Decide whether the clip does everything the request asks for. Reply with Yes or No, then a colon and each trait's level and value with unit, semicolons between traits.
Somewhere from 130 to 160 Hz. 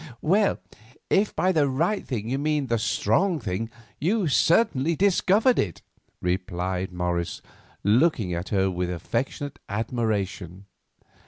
No: low, 115 Hz